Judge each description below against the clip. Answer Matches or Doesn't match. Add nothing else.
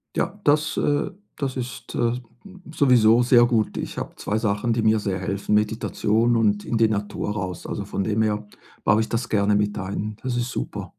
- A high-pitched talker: Doesn't match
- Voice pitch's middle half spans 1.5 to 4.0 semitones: Matches